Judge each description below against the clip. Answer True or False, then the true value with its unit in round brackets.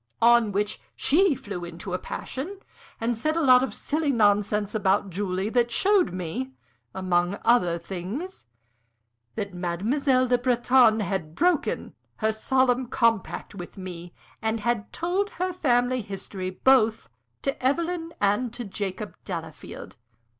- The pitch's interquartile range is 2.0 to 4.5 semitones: False (5.3 semitones)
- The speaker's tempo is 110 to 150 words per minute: True (135 wpm)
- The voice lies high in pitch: True (225 Hz)